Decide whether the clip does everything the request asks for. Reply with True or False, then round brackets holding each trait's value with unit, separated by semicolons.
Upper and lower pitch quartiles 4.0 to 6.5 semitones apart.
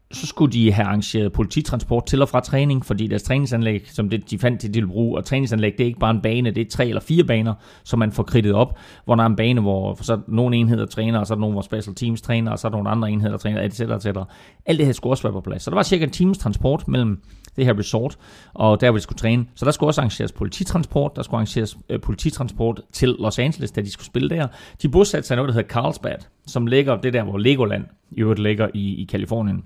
False (3.3 semitones)